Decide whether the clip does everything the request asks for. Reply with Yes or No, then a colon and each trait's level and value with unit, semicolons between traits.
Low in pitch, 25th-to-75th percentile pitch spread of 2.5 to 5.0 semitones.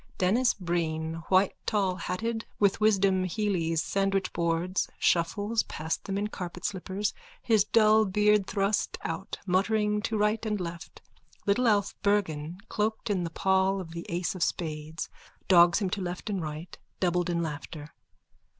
No: high, 190 Hz; average, 3.5 semitones